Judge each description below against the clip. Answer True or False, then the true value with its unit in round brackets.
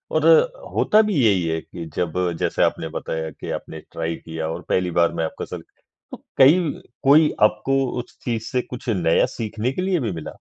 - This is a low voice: True (105 Hz)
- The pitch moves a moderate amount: False (7.8 semitones)